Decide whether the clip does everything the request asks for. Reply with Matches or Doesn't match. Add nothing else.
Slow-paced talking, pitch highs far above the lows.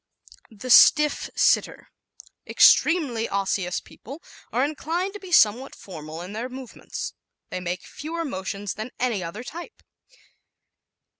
Matches